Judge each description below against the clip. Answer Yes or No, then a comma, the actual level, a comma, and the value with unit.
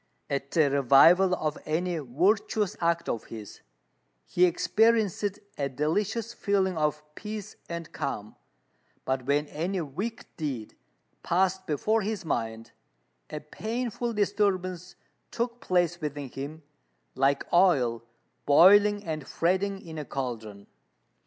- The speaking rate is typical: No, slow, 120 wpm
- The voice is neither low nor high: Yes, medium, 170 Hz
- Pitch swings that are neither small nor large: No, wide, 6.0 semitones